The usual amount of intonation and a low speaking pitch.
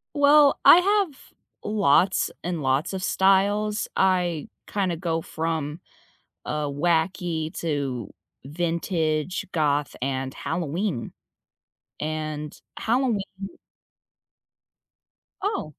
No: average, 4.5 semitones; medium, 170 Hz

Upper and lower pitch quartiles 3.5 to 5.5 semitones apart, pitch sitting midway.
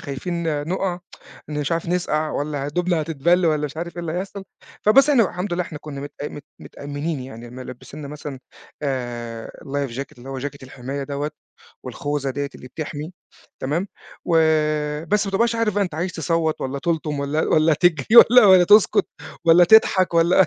Yes: average, 4.0 semitones; medium, 155 Hz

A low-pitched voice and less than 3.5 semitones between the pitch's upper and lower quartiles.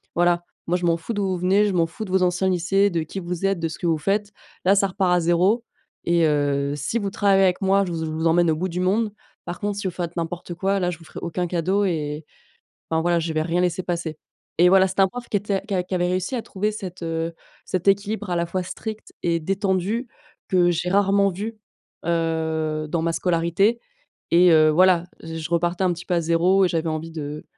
No: medium, 180 Hz; average, 2.8 semitones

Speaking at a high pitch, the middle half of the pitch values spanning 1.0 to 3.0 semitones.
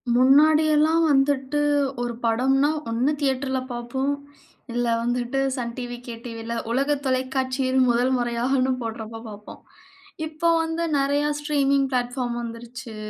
Yes: very high, 260 Hz; narrow, 2.6 semitones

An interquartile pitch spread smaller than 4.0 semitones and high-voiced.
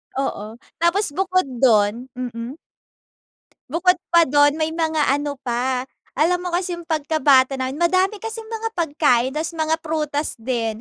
No: average, 4.9 semitones; very high, 305 Hz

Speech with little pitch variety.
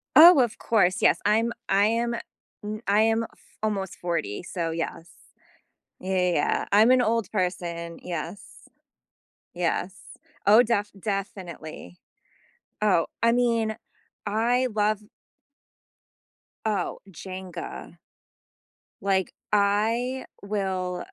No: average, 3.7 semitones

